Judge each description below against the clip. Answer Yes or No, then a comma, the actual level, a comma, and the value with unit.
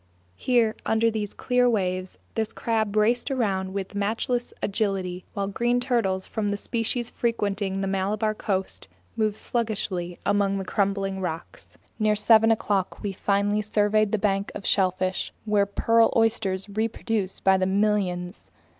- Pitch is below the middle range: No, high, 205 Hz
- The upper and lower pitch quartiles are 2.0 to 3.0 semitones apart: Yes, narrow, 2.5 semitones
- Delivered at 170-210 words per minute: No, average, 145 wpm